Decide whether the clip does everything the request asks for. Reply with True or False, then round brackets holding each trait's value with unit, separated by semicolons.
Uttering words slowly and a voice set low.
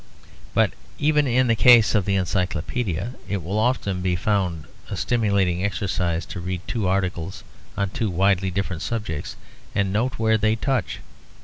False (155 wpm; 100 Hz)